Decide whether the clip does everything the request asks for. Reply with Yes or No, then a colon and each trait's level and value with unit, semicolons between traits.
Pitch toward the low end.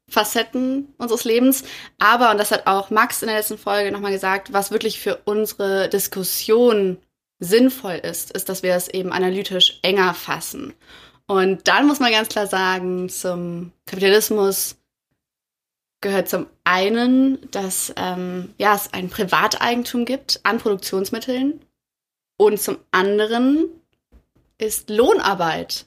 No: high, 205 Hz